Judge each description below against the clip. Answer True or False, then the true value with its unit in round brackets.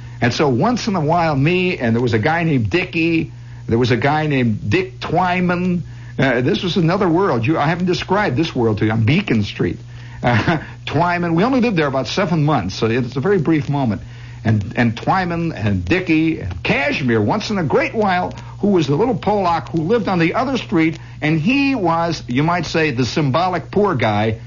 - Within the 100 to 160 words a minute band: False (205 wpm)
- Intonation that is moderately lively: False (6.1 semitones)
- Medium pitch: True (150 Hz)